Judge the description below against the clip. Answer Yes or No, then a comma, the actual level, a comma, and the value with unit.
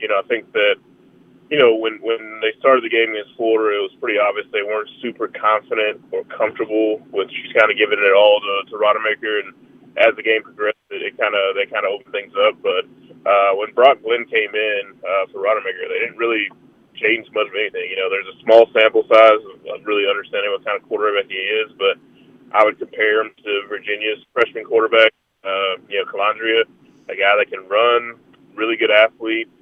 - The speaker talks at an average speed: No, fast, 210 wpm